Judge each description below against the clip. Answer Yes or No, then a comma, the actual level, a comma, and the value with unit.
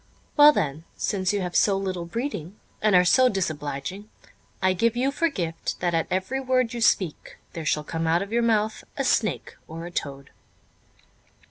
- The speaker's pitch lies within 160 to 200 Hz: Yes, high, 190 Hz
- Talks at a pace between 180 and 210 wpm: Yes, average, 185 wpm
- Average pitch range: No, wide, 5.9 semitones